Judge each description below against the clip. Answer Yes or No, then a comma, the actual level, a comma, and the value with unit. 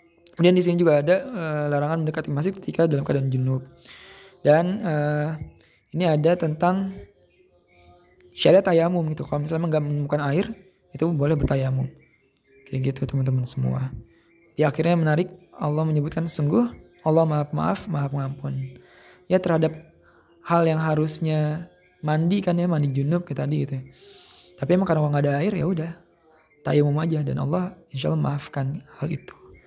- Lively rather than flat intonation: No, average, 3.4 semitones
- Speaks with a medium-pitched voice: Yes, medium, 155 Hz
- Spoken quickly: Yes, fast, 150 wpm